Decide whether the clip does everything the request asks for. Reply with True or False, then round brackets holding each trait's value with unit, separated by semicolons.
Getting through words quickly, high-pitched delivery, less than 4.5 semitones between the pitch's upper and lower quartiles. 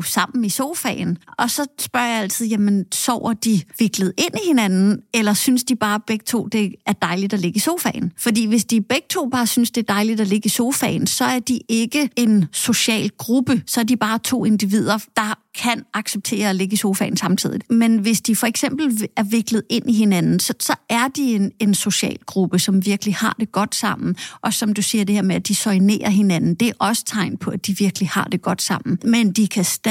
True (230 wpm; 220 Hz; 2.7 semitones)